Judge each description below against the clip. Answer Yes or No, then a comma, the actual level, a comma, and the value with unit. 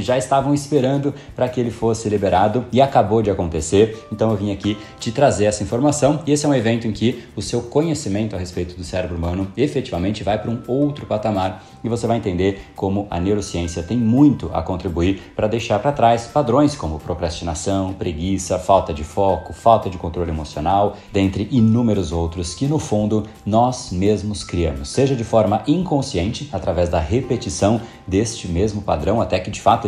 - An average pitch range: Yes, average, 4.2 semitones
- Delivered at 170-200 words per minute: Yes, average, 180 wpm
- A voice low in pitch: Yes, low, 105 Hz